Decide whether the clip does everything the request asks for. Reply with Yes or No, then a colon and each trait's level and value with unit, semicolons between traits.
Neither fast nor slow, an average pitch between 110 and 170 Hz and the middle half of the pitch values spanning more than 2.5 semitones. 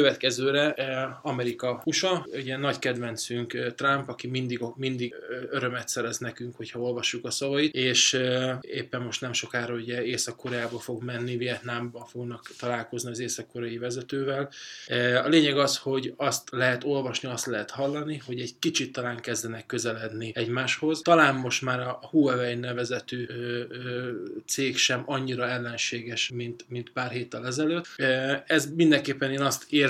No: average, 135 wpm; low, 125 Hz; narrow, 2.2 semitones